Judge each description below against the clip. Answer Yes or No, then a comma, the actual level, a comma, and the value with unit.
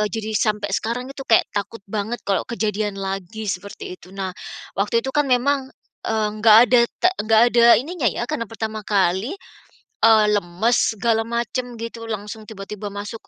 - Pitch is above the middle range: Yes, high, 220 Hz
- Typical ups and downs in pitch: No, narrow, 2.3 semitones